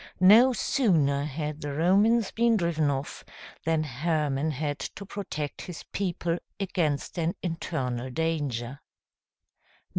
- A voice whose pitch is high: No, medium, 160 Hz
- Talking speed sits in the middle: No, slow, 115 wpm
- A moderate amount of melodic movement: Yes, average, 4.3 semitones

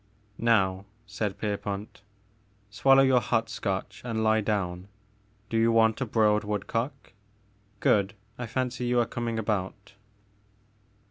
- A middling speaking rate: No, slow, 130 wpm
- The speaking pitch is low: Yes, low, 110 Hz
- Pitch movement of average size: No, narrow, 2.3 semitones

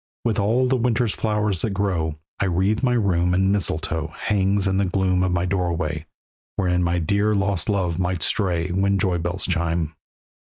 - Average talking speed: Yes, average, 180 wpm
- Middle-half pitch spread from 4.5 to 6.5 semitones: No, average, 2.8 semitones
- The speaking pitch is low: Yes, very low, 95 Hz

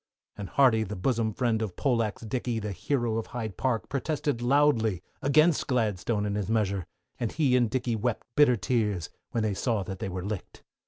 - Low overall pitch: Yes, low, 115 Hz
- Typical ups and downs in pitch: Yes, average, 3.5 semitones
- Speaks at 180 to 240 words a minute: Yes, average, 190 wpm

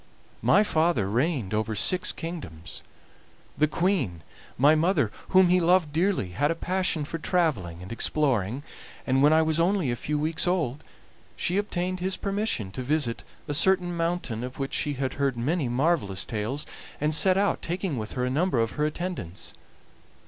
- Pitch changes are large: Yes, wide, 6.3 semitones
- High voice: No, medium, 150 Hz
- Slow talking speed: No, average, 170 wpm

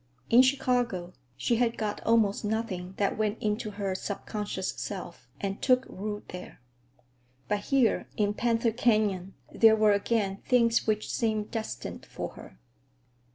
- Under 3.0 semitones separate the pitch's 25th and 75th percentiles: Yes, narrow, 2.5 semitones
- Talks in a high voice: Yes, high, 215 Hz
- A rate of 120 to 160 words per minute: Yes, average, 140 wpm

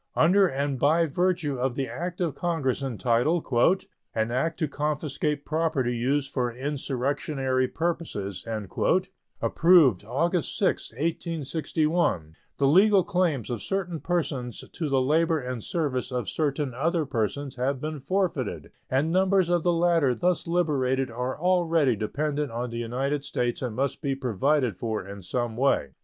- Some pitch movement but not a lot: Yes, average, 4.8 semitones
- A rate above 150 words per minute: No, average, 145 wpm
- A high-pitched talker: No, medium, 140 Hz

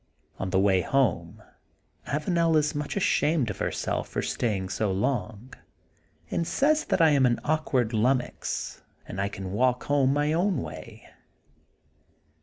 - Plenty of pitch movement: Yes, wide, 7.2 semitones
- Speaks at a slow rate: No, average, 145 wpm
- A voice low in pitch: Yes, low, 130 Hz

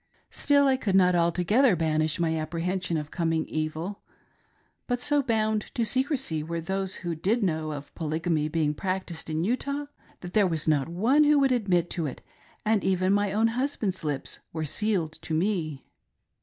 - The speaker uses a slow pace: No, average, 170 wpm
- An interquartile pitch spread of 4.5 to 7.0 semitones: Yes, wide, 5.4 semitones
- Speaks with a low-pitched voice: No, medium, 180 Hz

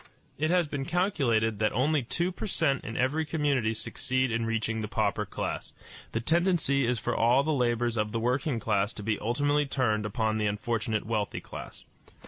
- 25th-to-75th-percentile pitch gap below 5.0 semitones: Yes, average, 4.6 semitones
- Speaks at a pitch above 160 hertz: No, low, 120 Hz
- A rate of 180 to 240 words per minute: Yes, average, 185 wpm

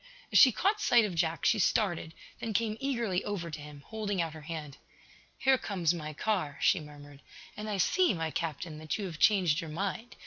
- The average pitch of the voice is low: No, medium, 175 Hz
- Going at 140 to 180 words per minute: No, fast, 205 wpm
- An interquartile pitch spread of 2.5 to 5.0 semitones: No, wide, 5.6 semitones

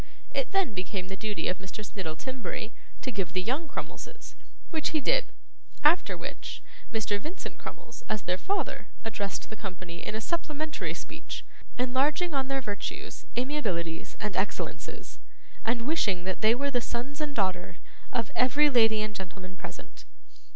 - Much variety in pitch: Yes, wide, 6.7 semitones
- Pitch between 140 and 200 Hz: No, high, 225 Hz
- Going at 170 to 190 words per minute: No, average, 160 wpm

